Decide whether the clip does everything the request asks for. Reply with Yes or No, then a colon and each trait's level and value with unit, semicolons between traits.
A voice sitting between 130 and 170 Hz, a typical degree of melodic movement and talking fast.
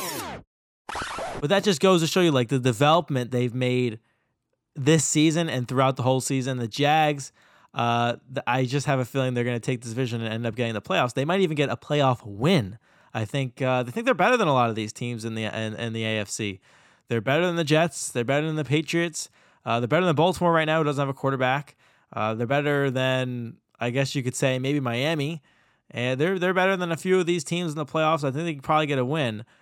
Yes: low, 135 Hz; average, 4.5 semitones; fast, 245 wpm